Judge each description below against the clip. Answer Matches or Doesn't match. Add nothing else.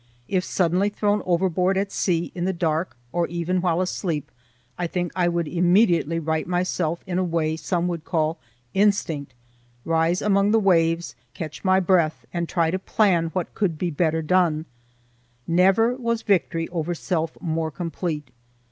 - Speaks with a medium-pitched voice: Matches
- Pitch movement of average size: Doesn't match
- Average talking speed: Matches